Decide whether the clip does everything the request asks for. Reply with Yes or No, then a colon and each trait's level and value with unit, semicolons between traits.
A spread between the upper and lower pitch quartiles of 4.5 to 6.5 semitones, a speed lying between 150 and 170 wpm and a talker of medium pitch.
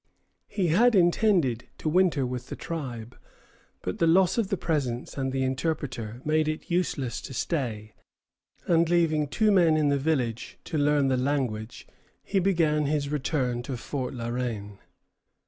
Yes: average, 5.0 semitones; average, 160 wpm; medium, 145 Hz